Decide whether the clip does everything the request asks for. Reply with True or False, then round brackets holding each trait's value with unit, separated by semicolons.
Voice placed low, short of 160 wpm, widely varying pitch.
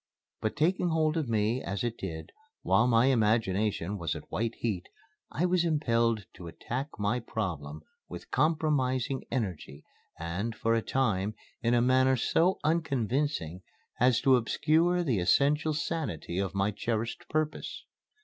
True (120 Hz; 145 wpm; 6.4 semitones)